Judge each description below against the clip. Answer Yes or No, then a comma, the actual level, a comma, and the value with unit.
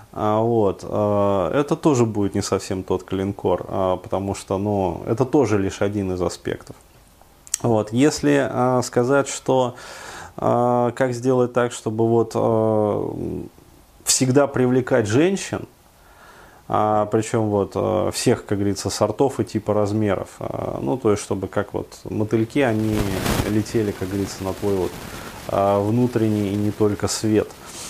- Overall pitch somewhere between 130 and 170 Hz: No, low, 110 Hz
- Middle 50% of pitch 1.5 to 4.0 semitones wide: Yes, average, 3.5 semitones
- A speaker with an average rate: Yes, average, 125 wpm